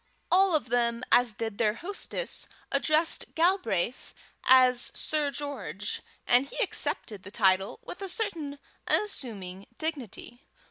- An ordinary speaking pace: No, slow, 125 wpm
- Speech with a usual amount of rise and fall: No, wide, 6.9 semitones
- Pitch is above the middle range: Yes, very high, 250 Hz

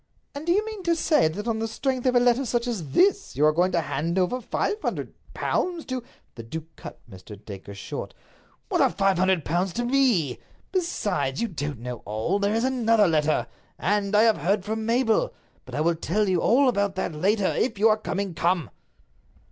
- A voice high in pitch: Yes, high, 205 Hz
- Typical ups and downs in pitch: No, wide, 6.9 semitones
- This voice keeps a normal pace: No, fast, 210 wpm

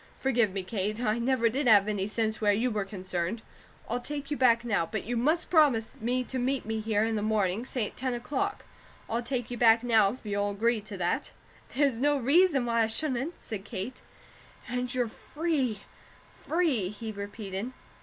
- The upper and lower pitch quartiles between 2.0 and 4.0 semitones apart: Yes, average, 3.4 semitones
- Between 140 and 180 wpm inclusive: No, average, 195 wpm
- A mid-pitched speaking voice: No, high, 230 Hz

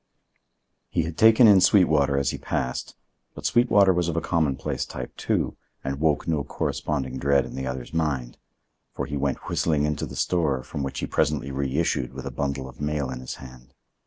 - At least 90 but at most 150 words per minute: No, average, 190 wpm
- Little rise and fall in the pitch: No, average, 3.5 semitones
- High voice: No, very low, 70 Hz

